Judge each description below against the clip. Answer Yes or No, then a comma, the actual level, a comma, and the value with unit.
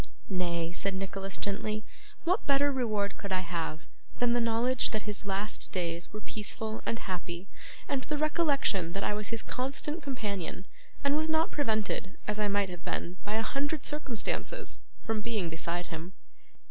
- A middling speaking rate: Yes, average, 170 wpm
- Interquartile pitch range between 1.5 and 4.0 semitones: No, wide, 5.5 semitones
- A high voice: Yes, high, 210 Hz